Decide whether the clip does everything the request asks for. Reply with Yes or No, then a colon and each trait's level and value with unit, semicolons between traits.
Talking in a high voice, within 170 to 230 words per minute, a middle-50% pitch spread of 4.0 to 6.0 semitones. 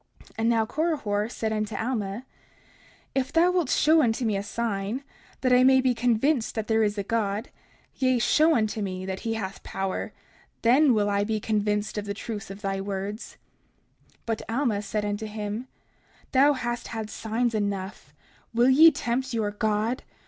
No: high, 220 Hz; average, 180 wpm; average, 3.4 semitones